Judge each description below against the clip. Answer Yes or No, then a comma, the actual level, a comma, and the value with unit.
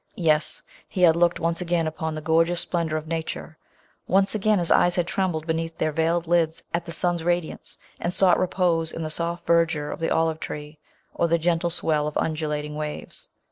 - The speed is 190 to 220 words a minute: Yes, average, 200 wpm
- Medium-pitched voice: Yes, medium, 165 Hz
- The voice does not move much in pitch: Yes, narrow, 1.7 semitones